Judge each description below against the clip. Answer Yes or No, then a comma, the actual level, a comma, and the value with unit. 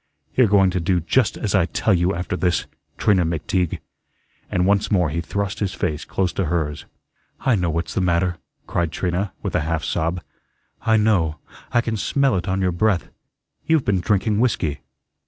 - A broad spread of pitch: No, average, 3.2 semitones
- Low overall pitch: Yes, very low, 90 Hz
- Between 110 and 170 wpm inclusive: No, average, 185 wpm